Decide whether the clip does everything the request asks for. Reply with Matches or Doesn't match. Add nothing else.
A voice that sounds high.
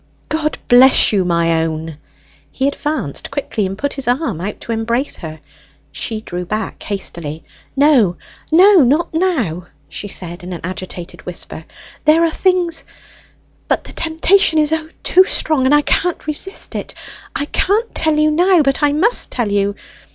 Matches